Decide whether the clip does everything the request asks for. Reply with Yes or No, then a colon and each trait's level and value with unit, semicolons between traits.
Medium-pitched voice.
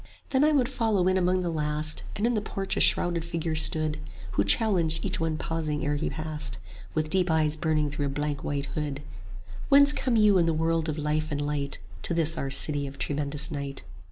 Yes: medium, 155 Hz